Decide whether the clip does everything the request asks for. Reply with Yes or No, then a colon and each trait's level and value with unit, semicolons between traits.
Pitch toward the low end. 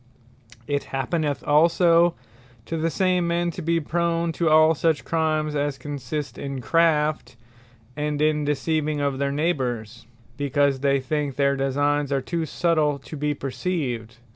No: medium, 150 Hz